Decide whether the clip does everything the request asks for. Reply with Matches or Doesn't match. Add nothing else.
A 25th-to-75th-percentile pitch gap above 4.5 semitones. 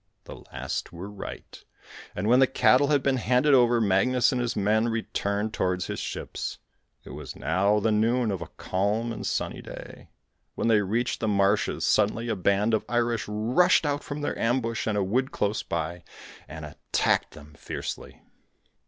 Doesn't match